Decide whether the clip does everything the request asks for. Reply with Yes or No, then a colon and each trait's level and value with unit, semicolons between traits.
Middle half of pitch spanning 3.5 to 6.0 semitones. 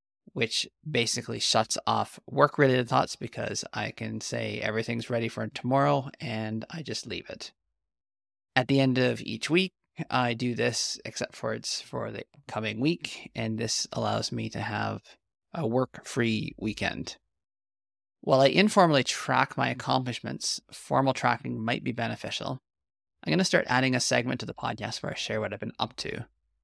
Yes: average, 3.8 semitones